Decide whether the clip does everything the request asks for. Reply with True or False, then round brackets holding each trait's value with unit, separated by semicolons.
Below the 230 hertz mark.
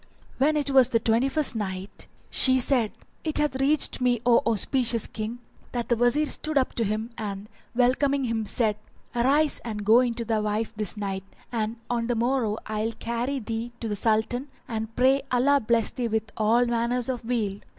False (235 Hz)